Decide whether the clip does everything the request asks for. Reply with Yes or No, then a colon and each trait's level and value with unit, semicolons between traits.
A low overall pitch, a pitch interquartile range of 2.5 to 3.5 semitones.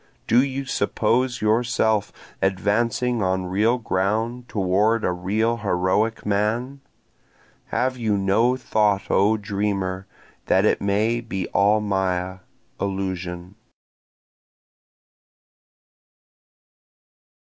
Yes: low, 105 Hz; average, 3.2 semitones